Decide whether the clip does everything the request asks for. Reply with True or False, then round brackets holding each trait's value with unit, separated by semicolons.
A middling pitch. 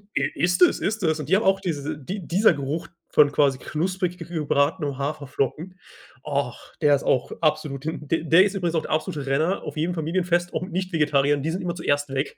True (160 Hz)